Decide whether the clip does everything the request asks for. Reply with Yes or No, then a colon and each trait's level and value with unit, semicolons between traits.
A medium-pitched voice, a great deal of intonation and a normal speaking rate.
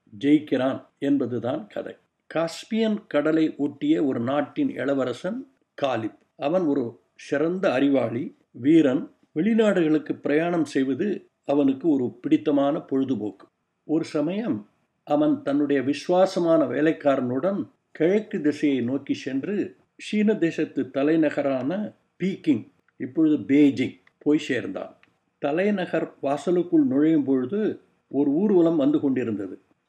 Yes: medium, 160 Hz; wide, 7.5 semitones; average, 95 wpm